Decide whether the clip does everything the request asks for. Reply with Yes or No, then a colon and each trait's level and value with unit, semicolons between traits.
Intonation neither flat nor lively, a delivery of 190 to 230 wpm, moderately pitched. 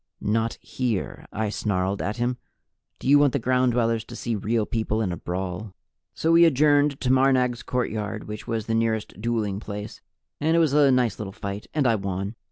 No: average, 3.7 semitones; average, 195 wpm; low, 115 Hz